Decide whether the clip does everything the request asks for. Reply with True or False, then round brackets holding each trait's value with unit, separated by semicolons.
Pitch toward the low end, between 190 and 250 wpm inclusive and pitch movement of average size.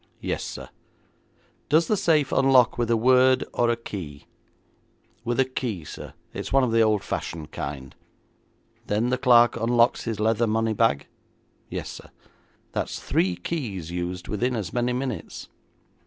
False (115 Hz; 155 wpm; 4.0 semitones)